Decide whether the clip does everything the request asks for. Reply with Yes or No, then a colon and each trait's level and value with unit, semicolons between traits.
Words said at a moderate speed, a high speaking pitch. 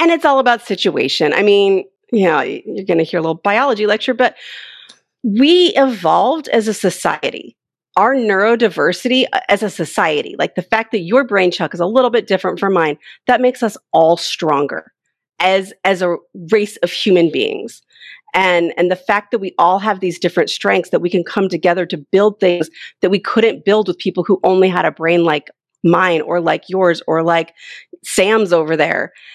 Yes: average, 190 wpm; high, 195 Hz